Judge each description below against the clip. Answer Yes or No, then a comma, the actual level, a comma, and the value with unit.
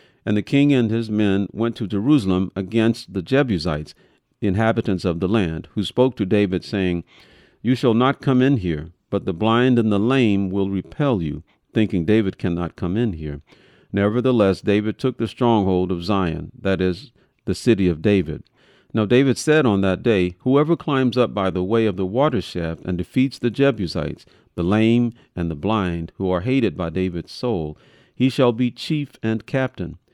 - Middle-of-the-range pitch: No, low, 105 Hz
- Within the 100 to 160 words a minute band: No, average, 185 wpm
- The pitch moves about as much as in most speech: Yes, average, 5.0 semitones